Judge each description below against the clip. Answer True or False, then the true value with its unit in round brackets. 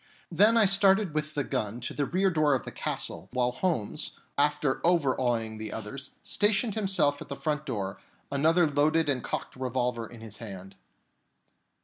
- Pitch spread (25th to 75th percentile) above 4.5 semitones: True (5.6 semitones)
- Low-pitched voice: False (145 Hz)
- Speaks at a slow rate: False (170 wpm)